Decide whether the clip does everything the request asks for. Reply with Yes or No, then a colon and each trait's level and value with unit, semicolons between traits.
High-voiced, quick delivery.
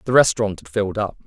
No: low, 105 Hz; fast, 235 wpm